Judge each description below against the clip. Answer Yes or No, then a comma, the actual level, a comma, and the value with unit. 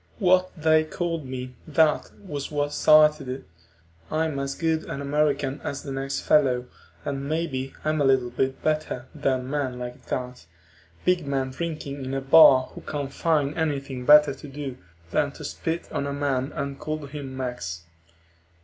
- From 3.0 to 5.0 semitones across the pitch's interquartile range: No, narrow, 2.6 semitones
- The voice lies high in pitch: No, medium, 140 Hz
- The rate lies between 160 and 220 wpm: Yes, average, 165 wpm